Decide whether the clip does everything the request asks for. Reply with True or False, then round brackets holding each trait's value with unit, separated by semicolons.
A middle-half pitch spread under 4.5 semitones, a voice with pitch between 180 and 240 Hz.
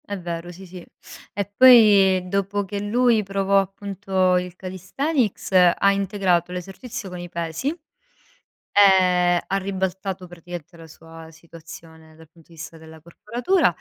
True (2.6 semitones; 185 Hz)